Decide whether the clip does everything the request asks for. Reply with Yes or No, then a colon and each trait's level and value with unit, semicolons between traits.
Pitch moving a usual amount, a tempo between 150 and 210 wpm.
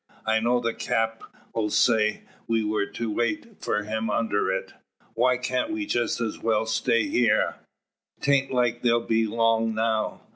No: narrow, 1.6 semitones; average, 155 wpm